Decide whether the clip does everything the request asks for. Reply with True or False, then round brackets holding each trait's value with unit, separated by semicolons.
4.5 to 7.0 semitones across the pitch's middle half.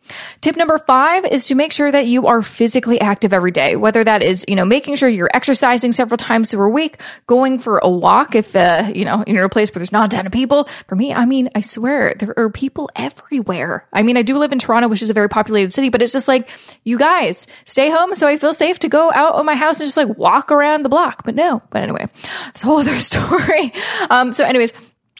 True (4.9 semitones)